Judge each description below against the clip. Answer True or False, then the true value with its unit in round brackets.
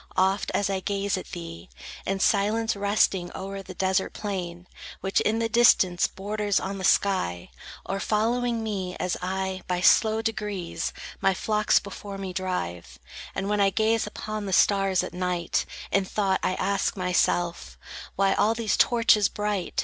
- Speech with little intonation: True (2.2 semitones)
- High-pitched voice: True (195 Hz)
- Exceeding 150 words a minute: True (160 wpm)